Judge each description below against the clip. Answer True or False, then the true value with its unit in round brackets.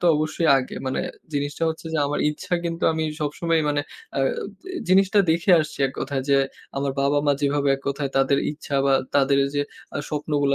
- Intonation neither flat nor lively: False (2.3 semitones)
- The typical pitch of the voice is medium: True (145 Hz)